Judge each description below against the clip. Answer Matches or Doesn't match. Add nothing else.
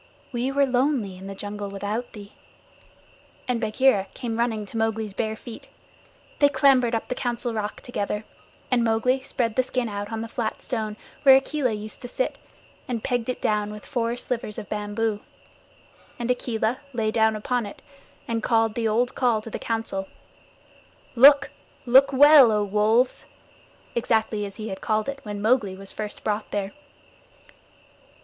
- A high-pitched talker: Matches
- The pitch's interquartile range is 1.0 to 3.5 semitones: Matches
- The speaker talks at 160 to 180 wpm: Matches